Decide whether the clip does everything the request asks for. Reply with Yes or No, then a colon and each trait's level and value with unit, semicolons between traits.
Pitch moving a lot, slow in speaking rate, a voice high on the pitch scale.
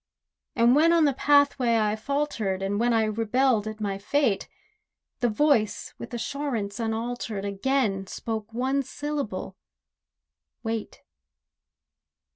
No: average, 4.5 semitones; slow, 110 wpm; high, 230 Hz